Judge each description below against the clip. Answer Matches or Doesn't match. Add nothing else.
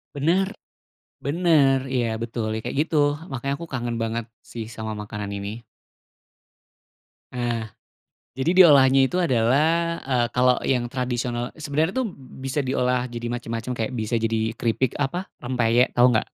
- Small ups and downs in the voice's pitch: Doesn't match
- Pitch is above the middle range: Doesn't match